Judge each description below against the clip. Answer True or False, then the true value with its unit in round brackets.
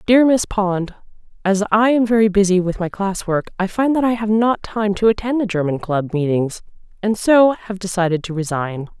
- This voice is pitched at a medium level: False (200 Hz)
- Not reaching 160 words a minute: False (205 wpm)